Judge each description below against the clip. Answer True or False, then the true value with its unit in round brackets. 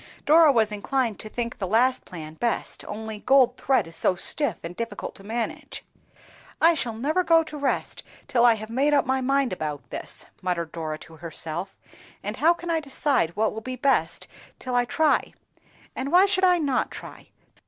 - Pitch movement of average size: False (5.7 semitones)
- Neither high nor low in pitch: False (245 Hz)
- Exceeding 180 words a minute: True (190 wpm)